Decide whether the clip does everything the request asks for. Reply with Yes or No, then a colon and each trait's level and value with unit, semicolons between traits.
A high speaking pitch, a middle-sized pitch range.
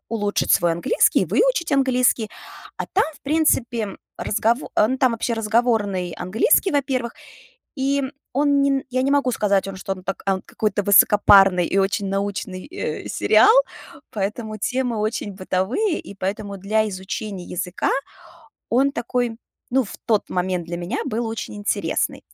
Yes: high, 215 Hz; average, 4.7 semitones